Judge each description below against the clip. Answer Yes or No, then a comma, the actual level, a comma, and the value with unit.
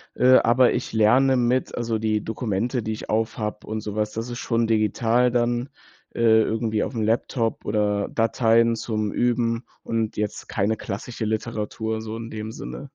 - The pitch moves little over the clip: Yes, narrow, 1.6 semitones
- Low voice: Yes, low, 115 Hz